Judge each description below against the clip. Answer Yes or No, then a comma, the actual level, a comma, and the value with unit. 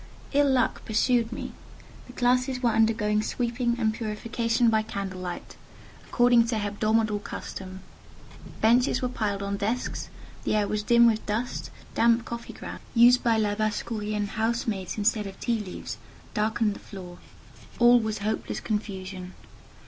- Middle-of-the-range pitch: No, high, 220 Hz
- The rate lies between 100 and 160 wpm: Yes, average, 140 wpm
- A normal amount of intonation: No, narrow, 2.3 semitones